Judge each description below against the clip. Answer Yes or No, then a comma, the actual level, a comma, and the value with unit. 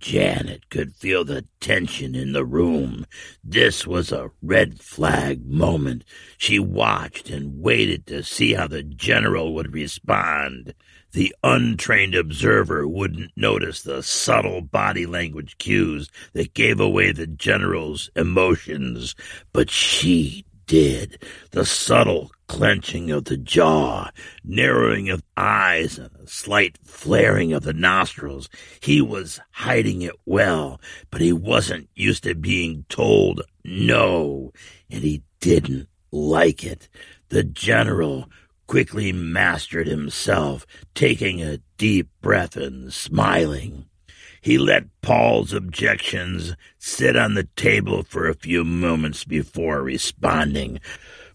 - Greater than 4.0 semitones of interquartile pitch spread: No, average, 3.2 semitones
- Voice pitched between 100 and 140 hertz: No, very low, 80 Hz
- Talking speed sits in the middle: No, slow, 120 wpm